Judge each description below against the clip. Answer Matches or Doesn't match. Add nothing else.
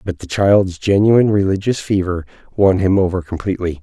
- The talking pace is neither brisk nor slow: Matches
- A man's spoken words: Matches